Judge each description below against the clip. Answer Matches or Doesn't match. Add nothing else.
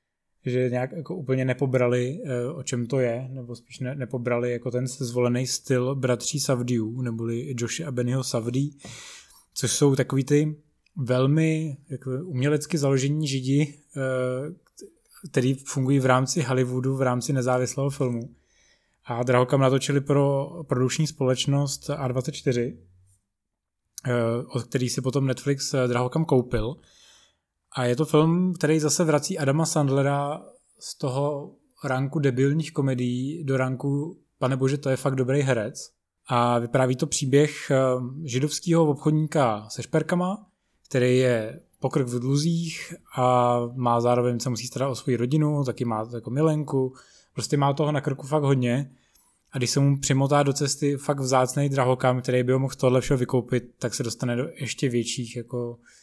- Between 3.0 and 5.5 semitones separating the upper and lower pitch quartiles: Doesn't match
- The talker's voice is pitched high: Doesn't match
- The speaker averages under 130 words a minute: Doesn't match